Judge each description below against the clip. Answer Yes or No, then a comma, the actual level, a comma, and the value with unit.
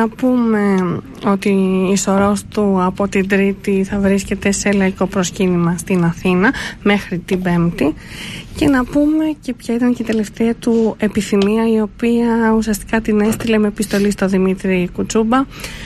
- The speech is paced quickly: No, average, 150 wpm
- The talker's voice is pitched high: Yes, high, 205 Hz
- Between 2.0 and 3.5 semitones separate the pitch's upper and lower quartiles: Yes, average, 2.7 semitones